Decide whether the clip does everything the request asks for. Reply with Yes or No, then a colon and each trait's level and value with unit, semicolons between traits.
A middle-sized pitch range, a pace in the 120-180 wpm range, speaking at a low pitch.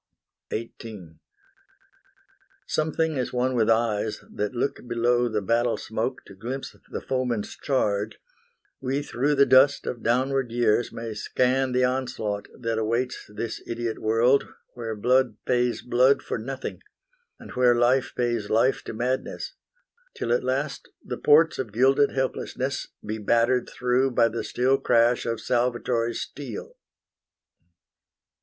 No: narrow, 2.3 semitones; slow, 135 wpm; low, 120 Hz